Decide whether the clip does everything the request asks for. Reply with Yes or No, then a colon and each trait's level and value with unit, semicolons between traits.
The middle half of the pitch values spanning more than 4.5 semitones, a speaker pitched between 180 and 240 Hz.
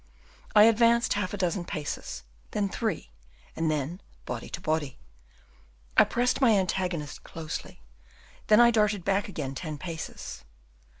Yes: average, 5.3 semitones; medium, 185 Hz